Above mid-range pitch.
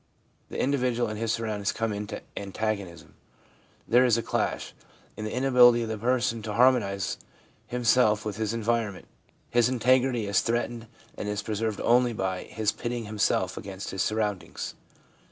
No: low, 110 Hz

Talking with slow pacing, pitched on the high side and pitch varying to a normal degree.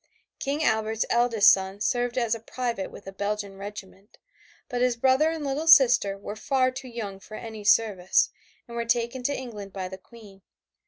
No: average, 175 wpm; high, 230 Hz; average, 3.7 semitones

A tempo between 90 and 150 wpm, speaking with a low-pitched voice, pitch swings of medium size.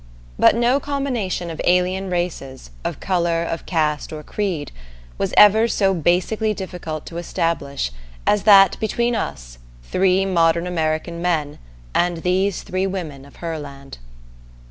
No: slow, 135 wpm; medium, 175 Hz; average, 3.6 semitones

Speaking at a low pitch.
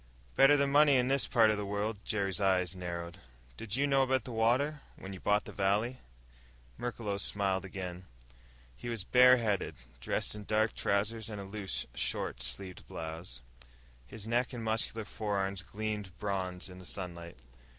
Yes: low, 105 Hz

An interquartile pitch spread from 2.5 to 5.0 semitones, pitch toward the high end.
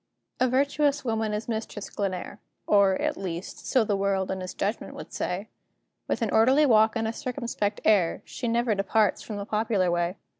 Yes: average, 3.0 semitones; high, 215 Hz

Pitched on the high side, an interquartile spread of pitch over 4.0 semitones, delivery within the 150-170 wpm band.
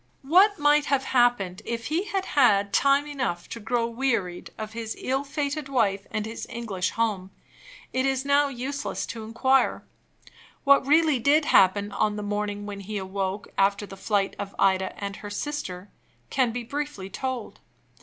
Yes: high, 230 Hz; wide, 5.5 semitones; average, 165 wpm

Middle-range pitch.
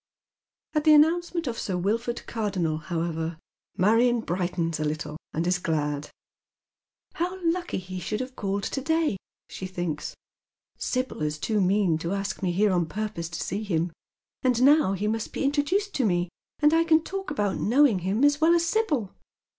No: high, 210 Hz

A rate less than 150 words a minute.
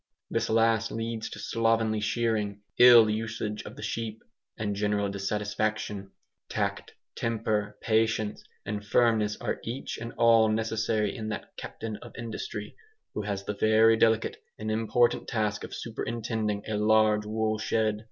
Yes: average, 140 wpm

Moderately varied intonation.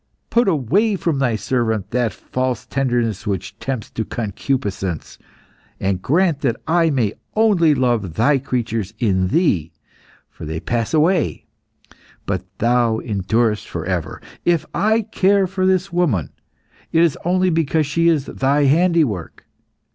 No: wide, 7.5 semitones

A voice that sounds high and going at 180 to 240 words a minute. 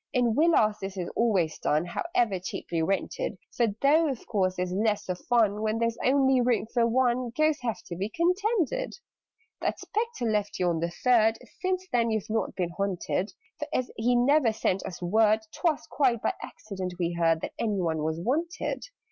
Yes: high, 220 Hz; average, 190 wpm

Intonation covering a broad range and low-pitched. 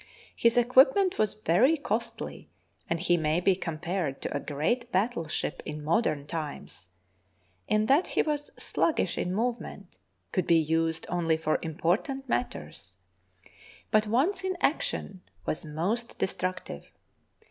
No: wide, 6.9 semitones; medium, 185 Hz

